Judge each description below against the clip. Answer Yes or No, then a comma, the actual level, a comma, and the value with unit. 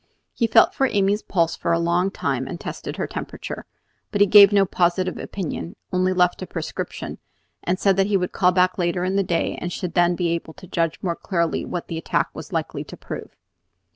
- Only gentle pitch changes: Yes, narrow, 2.3 semitones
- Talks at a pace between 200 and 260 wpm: Yes, fast, 205 wpm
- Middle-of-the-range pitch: Yes, medium, 180 Hz